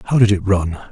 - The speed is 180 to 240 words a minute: No, fast, 260 wpm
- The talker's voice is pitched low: Yes, low, 100 Hz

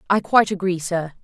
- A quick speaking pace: No, average, 195 wpm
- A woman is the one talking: Yes, female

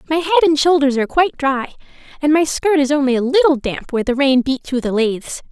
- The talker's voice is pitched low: No, very high, 285 Hz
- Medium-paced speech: No, fast, 240 wpm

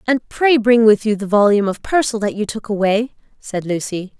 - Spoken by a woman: Yes, female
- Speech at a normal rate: No, fast, 215 wpm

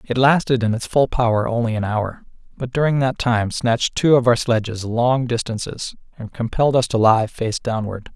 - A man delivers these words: Yes, male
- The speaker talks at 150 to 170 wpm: No, average, 200 wpm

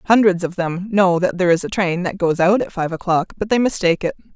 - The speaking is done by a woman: Yes, female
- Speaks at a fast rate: Yes, fast, 260 wpm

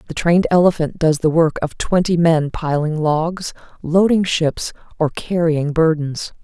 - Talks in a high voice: No, medium, 160 Hz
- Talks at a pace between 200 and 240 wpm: No, average, 150 wpm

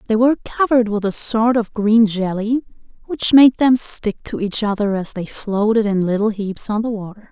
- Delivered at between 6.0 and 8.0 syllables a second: No, 5.0 syllables/s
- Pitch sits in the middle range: No, high, 215 Hz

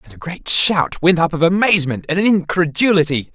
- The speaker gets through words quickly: No, average, 180 wpm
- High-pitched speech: No, medium, 170 Hz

